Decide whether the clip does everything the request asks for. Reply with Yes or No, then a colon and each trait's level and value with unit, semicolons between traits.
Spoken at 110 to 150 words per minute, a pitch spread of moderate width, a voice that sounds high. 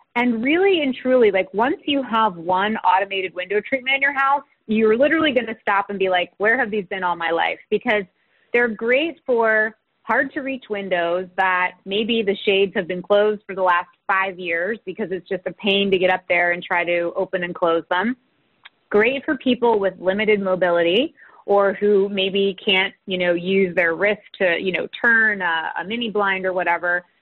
No: average, 200 wpm; average, 3.8 semitones; high, 200 Hz